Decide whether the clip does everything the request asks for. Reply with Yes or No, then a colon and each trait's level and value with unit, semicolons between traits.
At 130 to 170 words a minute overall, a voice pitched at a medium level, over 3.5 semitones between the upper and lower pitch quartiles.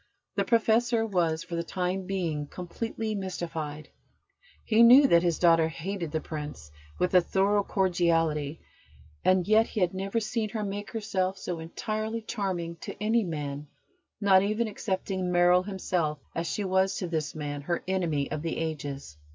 Yes: average, 160 wpm; medium, 180 Hz; average, 3.9 semitones